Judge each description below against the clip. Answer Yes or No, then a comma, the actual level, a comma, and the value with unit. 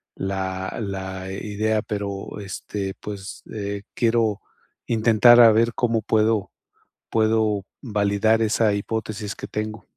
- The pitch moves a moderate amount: No, narrow, 1.9 semitones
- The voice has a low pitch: Yes, low, 105 Hz